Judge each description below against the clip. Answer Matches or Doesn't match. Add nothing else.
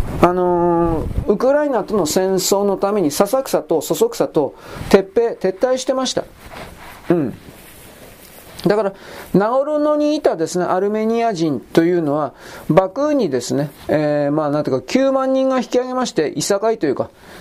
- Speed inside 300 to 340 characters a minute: Doesn't match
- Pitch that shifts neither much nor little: Doesn't match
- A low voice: Doesn't match